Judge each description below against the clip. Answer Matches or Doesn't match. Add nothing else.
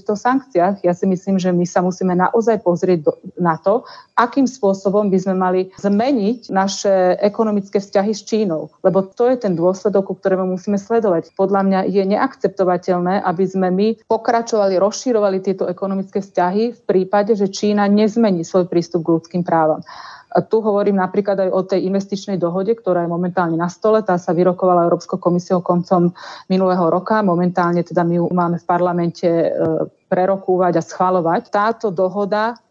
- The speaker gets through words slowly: Doesn't match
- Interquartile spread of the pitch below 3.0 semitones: Matches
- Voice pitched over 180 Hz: Matches